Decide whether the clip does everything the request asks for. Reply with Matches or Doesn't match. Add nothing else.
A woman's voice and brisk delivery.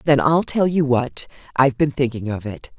Matches